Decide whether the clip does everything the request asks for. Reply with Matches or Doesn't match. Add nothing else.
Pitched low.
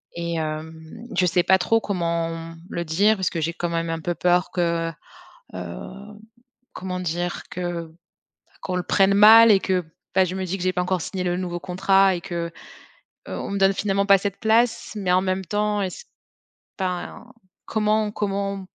Doesn't match